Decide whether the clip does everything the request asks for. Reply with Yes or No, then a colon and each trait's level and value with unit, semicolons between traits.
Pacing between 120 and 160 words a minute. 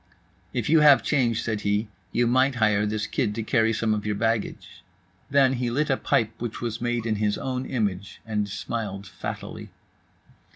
No: average, 180 wpm